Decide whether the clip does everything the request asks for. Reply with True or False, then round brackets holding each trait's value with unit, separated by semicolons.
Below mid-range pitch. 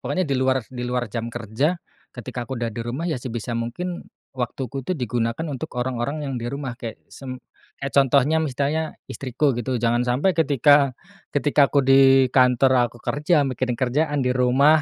True (130 Hz)